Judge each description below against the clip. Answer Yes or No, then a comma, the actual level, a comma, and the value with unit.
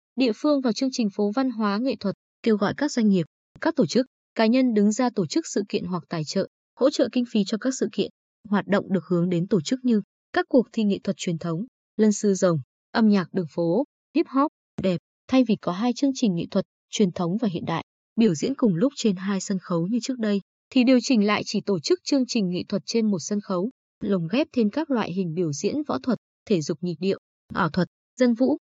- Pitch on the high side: Yes, high, 210 Hz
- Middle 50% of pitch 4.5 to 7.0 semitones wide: Yes, average, 4.8 semitones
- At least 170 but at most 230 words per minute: No, fast, 250 wpm